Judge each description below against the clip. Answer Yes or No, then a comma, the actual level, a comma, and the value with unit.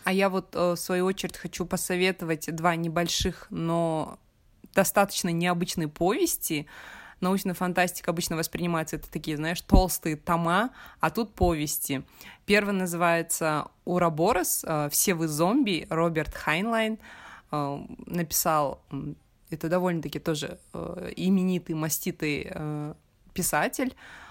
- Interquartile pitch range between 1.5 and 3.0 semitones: Yes, average, 2.7 semitones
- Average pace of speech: No, slow, 100 wpm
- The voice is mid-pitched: Yes, medium, 175 Hz